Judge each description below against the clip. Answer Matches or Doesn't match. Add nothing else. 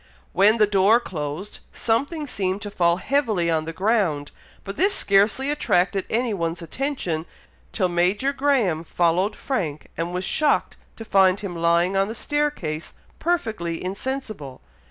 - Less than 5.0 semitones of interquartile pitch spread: Doesn't match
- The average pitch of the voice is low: Doesn't match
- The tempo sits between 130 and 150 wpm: Matches